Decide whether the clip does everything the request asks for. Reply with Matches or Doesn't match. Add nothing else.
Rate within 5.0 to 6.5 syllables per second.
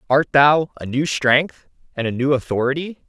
Doesn't match